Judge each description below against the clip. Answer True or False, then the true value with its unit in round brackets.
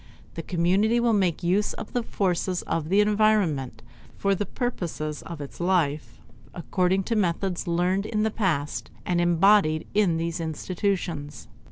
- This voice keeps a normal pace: True (150 wpm)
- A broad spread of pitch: False (3.7 semitones)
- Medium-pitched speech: True (180 Hz)